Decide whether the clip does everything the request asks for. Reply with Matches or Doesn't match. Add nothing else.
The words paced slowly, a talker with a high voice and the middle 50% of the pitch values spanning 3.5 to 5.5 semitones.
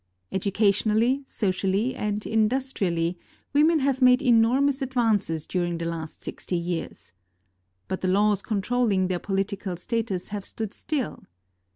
Matches